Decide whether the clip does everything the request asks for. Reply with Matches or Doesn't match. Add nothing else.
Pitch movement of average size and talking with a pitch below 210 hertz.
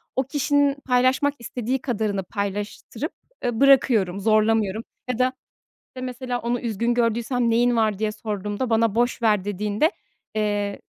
Doesn't match